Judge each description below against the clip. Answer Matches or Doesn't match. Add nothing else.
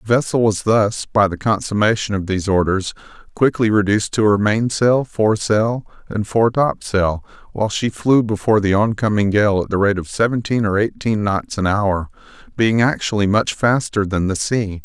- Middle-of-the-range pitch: Doesn't match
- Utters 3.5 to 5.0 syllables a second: Doesn't match